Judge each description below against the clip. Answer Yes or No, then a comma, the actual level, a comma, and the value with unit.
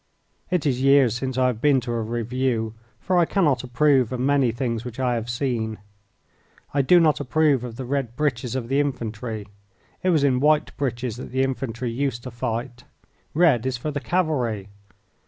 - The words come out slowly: No, average, 190 wpm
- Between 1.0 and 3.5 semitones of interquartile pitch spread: Yes, average, 3.2 semitones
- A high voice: No, low, 130 Hz